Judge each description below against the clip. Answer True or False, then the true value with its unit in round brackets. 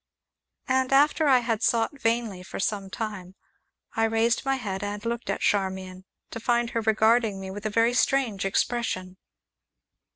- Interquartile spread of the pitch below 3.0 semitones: False (3.5 semitones)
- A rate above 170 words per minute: False (160 wpm)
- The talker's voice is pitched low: False (225 Hz)